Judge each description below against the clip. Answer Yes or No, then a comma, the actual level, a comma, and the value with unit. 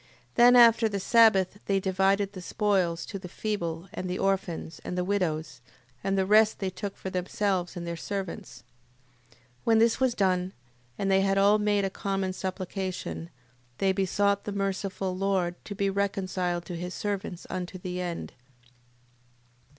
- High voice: Yes, high, 195 Hz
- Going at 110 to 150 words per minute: No, average, 165 wpm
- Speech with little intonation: Yes, narrow, 1.9 semitones